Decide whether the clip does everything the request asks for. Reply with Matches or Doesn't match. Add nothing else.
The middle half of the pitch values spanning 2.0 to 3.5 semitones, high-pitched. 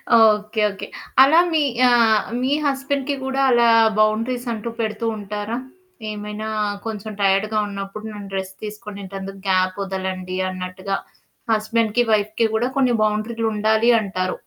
Matches